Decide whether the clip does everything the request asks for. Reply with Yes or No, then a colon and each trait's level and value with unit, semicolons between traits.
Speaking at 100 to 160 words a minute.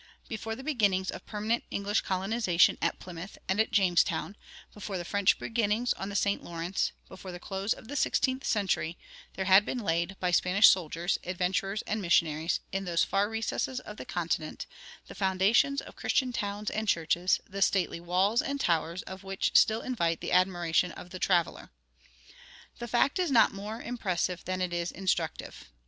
No: average, 175 wpm